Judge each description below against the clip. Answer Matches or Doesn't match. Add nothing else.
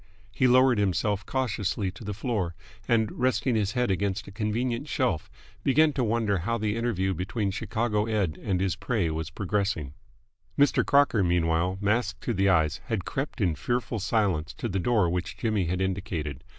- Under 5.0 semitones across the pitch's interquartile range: Matches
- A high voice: Doesn't match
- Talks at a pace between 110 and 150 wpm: Doesn't match